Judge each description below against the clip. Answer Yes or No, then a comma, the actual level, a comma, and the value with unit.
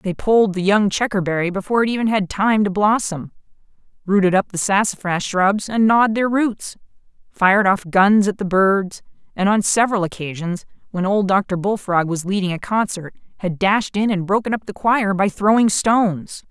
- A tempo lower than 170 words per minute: No, average, 180 wpm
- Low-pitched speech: No, high, 200 Hz